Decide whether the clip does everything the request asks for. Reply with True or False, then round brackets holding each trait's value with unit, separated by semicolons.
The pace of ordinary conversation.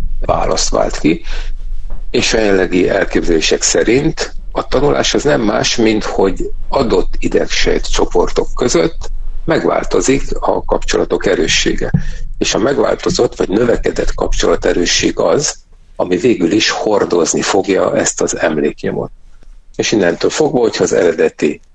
True (125 wpm)